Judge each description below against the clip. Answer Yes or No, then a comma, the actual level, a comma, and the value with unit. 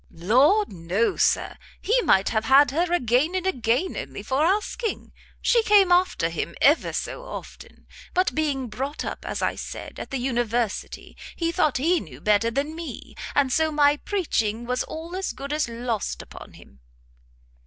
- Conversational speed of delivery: Yes, average, 170 wpm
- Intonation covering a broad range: Yes, wide, 6.8 semitones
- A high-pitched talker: Yes, very high, 280 Hz